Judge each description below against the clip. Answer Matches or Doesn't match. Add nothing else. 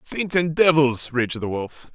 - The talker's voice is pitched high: Doesn't match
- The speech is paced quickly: Doesn't match